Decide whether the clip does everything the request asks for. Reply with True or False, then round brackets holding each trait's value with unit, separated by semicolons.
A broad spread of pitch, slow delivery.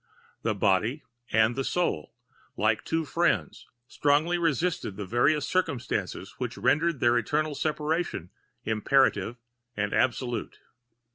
True (6.2 semitones; 115 wpm)